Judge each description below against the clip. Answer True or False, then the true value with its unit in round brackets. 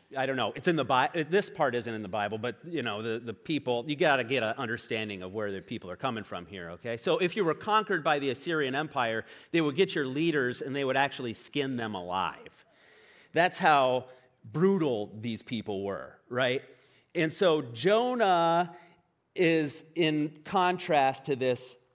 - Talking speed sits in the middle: True (190 wpm)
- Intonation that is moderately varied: False (5.9 semitones)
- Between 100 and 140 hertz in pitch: True (135 Hz)